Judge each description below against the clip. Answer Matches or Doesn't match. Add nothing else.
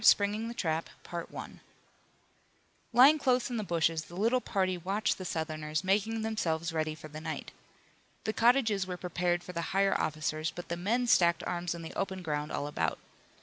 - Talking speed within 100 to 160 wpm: Doesn't match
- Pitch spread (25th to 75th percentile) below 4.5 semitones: Doesn't match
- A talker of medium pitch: Matches